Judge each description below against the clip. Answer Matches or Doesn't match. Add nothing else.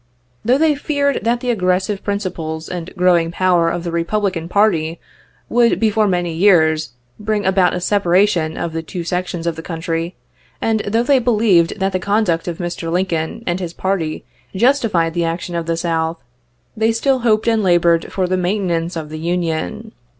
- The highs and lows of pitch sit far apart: Doesn't match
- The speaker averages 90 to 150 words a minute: Doesn't match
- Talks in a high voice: Doesn't match